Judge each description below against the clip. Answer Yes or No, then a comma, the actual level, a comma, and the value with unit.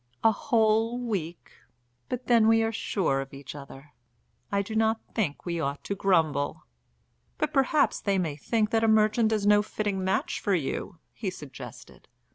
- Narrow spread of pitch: No, wide, 5.5 semitones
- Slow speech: No, average, 170 wpm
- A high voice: Yes, high, 205 Hz